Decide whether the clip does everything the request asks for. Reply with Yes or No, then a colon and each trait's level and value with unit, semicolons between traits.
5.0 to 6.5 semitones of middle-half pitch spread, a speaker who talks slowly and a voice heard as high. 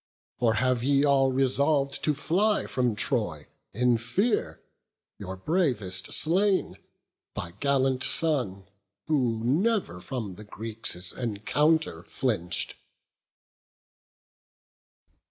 No: wide, 5.6 semitones; slow, 95 wpm; low, 130 Hz